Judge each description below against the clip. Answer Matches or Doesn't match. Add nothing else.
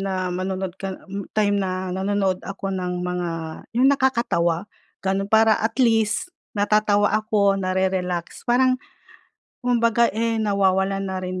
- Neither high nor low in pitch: Doesn't match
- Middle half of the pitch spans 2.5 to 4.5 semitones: Matches